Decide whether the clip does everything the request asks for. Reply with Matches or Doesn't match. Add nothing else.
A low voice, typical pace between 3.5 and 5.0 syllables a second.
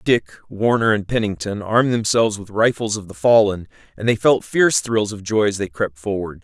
Doesn't match